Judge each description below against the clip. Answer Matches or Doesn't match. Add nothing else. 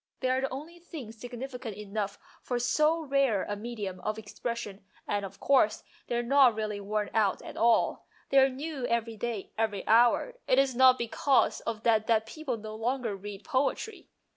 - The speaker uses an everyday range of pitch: Matches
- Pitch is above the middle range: Matches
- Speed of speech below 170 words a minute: Doesn't match